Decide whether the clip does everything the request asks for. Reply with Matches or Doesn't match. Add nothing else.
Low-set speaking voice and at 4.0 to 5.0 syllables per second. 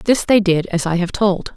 Doesn't match